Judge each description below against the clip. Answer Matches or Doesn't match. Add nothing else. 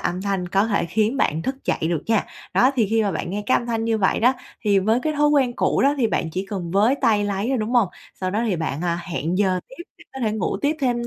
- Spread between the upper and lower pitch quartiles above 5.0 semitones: Doesn't match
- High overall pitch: Matches